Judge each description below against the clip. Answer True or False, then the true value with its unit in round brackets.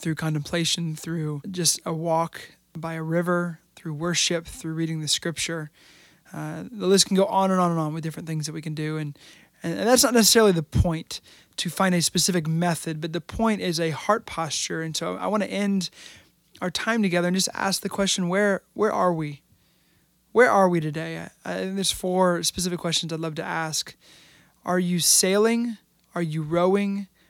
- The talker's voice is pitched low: False (175 Hz)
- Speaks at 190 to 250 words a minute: True (195 wpm)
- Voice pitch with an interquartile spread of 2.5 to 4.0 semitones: True (2.9 semitones)